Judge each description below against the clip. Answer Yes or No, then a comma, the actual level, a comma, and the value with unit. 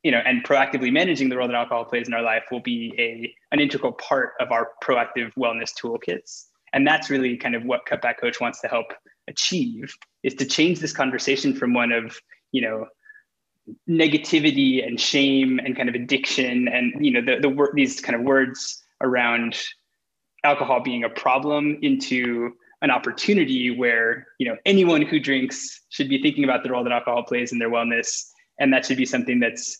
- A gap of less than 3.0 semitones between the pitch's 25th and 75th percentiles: No, average, 4.3 semitones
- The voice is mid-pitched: No, low, 130 Hz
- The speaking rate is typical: Yes, average, 190 wpm